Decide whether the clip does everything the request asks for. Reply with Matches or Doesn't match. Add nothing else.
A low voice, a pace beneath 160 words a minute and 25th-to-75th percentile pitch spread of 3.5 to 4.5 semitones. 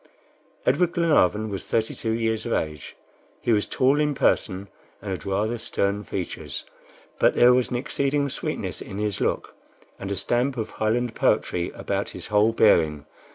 Doesn't match